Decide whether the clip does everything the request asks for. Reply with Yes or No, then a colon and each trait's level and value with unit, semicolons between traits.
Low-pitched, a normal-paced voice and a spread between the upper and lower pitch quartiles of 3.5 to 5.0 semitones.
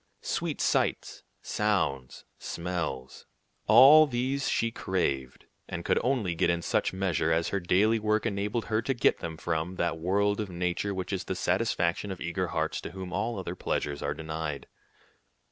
Yes: very low, 95 Hz; average, 165 wpm; average, 4.2 semitones